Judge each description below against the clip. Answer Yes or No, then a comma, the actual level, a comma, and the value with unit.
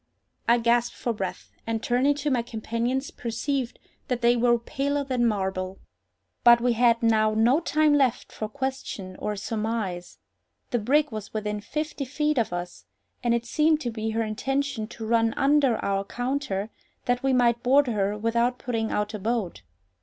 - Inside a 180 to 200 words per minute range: No, average, 170 wpm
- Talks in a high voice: Yes, high, 235 Hz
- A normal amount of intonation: Yes, average, 3.4 semitones